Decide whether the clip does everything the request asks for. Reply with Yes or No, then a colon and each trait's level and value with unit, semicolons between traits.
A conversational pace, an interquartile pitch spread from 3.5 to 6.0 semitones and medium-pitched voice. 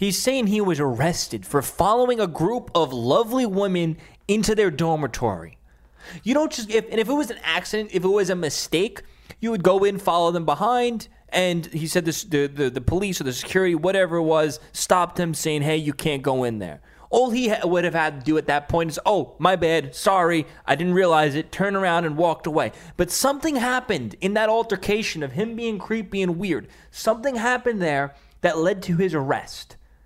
No: fast, 210 wpm; average, 5.2 semitones; medium, 175 Hz